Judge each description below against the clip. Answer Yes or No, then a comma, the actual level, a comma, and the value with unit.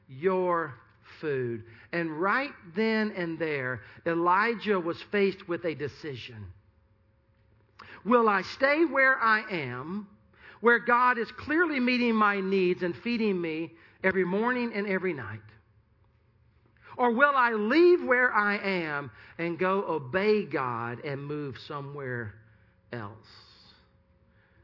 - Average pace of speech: No, slow, 120 wpm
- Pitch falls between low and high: Yes, medium, 170 Hz